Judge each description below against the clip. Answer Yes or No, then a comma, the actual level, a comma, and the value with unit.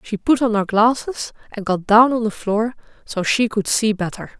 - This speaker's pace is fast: Yes, fast, 220 wpm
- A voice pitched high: Yes, high, 220 Hz